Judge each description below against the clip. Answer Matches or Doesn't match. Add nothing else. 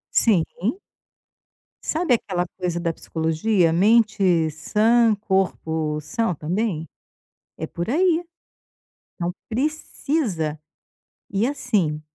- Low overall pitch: Doesn't match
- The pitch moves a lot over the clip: Matches